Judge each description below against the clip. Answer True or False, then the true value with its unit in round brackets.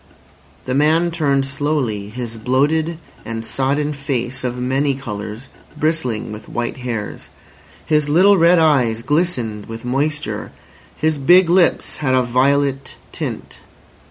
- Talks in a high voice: False (135 Hz)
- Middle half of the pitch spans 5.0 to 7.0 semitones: False (4.2 semitones)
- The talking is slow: True (130 wpm)